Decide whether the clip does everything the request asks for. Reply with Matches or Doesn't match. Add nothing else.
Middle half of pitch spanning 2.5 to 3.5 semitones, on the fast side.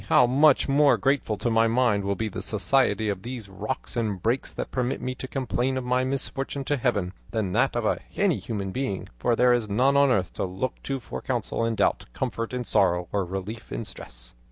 Doesn't match